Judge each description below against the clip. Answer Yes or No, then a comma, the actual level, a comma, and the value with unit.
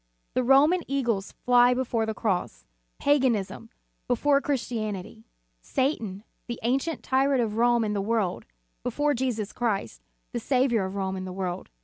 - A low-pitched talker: No, high, 235 Hz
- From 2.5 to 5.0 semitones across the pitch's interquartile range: Yes, average, 4.7 semitones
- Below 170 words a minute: Yes, average, 150 wpm